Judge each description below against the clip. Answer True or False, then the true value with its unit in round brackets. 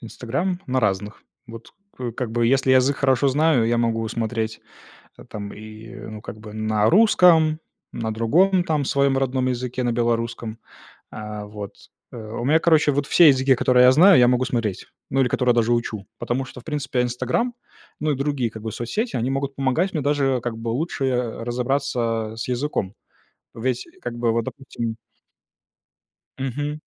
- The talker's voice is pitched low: True (125 Hz)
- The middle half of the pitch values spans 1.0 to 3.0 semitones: False (3.4 semitones)